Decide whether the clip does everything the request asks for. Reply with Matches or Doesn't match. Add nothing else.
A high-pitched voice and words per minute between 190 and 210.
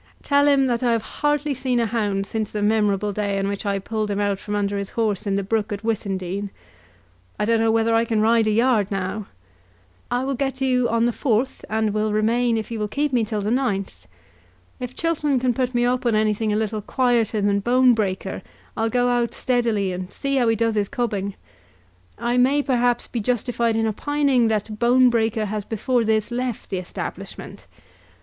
Matches